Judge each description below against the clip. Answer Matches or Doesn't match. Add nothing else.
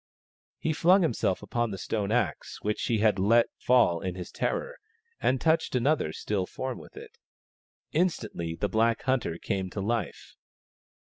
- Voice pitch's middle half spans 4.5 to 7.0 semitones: Matches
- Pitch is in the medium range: Doesn't match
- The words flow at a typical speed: Matches